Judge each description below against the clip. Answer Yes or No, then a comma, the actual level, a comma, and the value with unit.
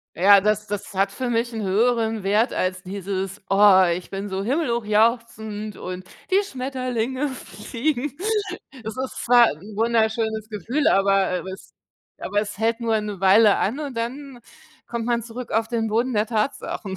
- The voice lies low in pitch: No, high, 220 Hz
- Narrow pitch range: No, average, 3.0 semitones